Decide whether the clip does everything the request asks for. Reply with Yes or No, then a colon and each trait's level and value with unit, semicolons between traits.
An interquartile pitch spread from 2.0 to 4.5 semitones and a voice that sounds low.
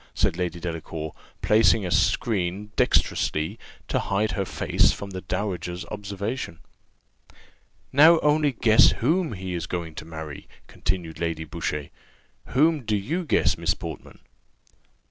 No: average, 5.3 semitones; very low, 95 Hz